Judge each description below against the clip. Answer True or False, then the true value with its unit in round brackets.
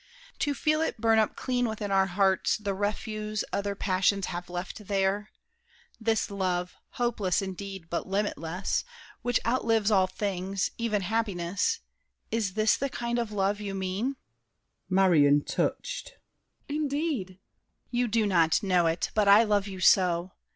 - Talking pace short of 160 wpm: True (145 wpm)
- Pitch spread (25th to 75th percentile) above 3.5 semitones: False (3.1 semitones)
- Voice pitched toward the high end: True (200 Hz)